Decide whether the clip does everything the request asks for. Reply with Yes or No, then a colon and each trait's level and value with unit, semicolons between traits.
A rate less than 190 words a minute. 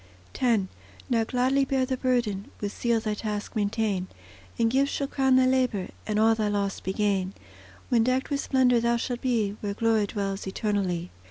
Yes: average, 180 wpm